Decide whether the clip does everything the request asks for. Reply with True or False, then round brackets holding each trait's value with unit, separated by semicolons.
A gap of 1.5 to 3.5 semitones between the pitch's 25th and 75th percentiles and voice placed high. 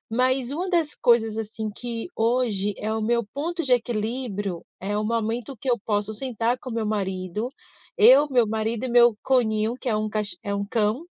True (2.9 semitones; 225 Hz)